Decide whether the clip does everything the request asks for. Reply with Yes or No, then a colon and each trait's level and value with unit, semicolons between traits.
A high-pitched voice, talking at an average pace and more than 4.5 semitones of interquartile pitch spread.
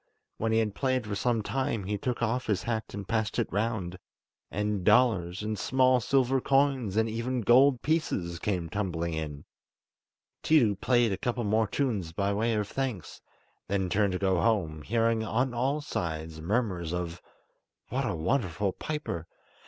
No: low, 110 Hz; average, 165 wpm; average, 4.9 semitones